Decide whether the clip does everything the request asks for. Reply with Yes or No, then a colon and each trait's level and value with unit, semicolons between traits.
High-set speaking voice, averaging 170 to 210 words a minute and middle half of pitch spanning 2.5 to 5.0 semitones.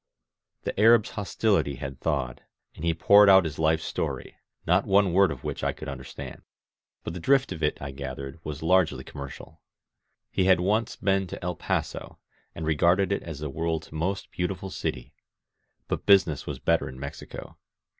No: very low, 85 Hz; average, 175 wpm; average, 4.7 semitones